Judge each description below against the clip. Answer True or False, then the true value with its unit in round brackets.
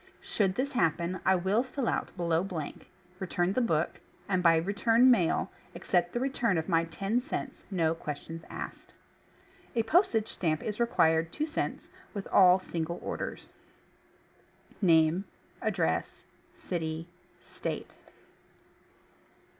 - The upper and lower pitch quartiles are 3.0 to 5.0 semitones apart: False (5.5 semitones)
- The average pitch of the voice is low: False (185 Hz)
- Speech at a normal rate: False (125 wpm)